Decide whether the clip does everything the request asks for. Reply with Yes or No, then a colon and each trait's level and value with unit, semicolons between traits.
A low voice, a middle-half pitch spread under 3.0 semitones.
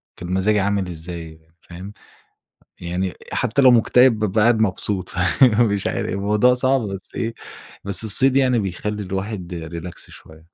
No: low, 100 Hz; average, 3.9 semitones